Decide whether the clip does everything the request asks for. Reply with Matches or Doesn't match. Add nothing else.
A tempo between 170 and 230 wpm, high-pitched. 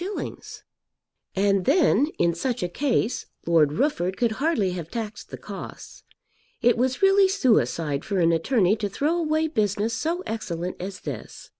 Doesn't match